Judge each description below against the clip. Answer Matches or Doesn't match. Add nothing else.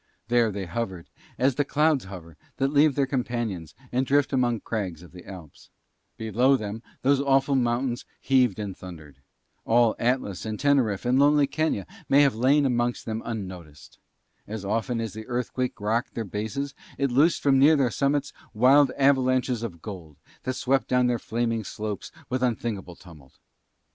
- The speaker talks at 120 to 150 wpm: Doesn't match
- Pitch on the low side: Matches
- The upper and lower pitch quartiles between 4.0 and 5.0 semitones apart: Matches